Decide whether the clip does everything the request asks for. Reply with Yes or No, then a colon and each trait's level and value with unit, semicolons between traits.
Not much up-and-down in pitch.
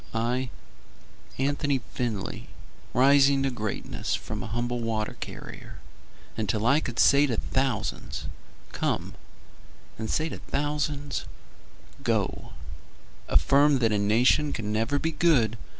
No: average, 4.1 semitones